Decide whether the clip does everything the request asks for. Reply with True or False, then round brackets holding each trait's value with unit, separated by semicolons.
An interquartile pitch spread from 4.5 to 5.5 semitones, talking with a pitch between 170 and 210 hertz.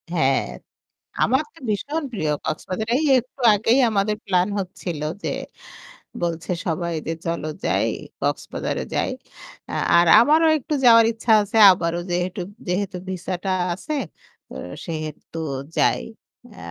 True (4.9 semitones; 185 Hz)